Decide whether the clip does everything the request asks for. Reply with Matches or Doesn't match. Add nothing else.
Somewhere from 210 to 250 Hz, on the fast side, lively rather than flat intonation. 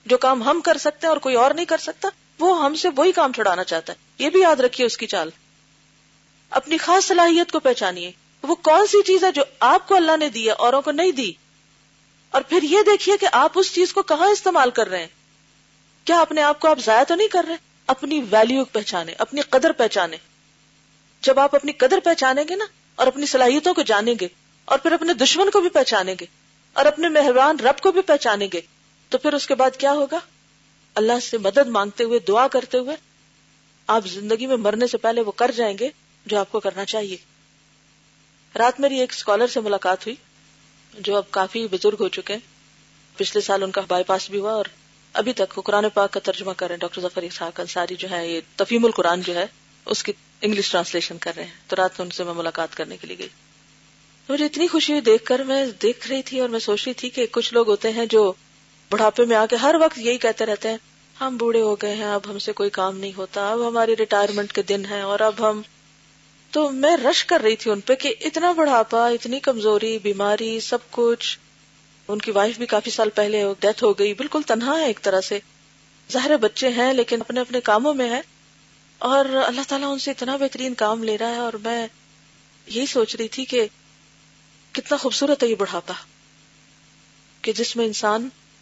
Matches